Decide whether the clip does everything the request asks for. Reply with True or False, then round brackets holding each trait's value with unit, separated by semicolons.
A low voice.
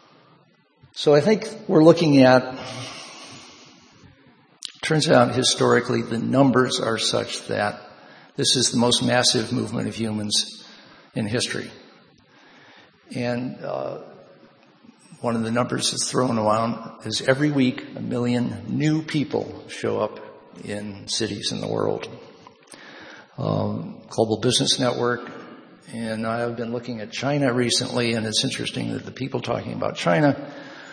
True (125 Hz)